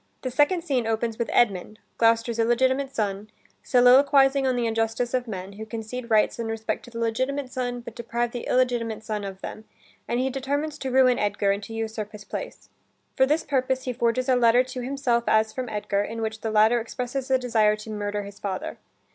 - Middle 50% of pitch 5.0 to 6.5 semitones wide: No, average, 2.8 semitones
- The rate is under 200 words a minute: No, fast, 205 wpm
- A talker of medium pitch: No, high, 235 Hz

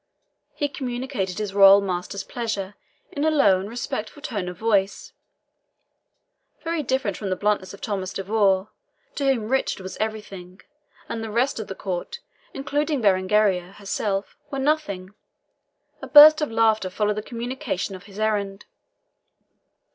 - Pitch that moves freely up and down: No, average, 4.7 semitones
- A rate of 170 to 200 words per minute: No, average, 145 wpm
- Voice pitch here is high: Yes, high, 210 Hz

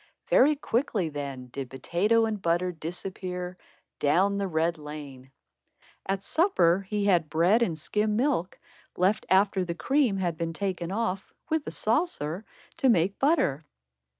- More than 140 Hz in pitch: Yes, medium, 185 Hz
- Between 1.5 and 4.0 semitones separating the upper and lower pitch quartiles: No, average, 4.5 semitones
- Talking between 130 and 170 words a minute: Yes, average, 145 wpm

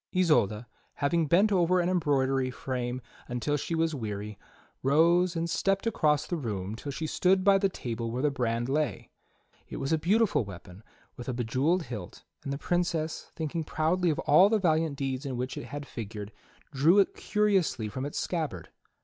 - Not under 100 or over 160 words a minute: No, average, 180 wpm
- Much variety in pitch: Yes, wide, 5.7 semitones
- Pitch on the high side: No, medium, 145 Hz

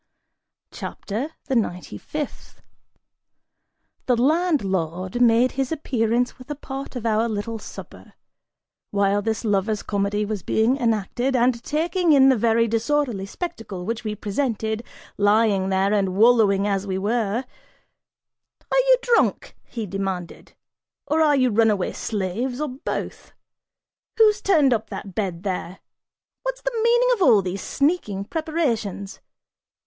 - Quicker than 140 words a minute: No, slow, 135 wpm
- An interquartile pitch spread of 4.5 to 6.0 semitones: Yes, average, 5.2 semitones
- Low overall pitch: No, high, 225 Hz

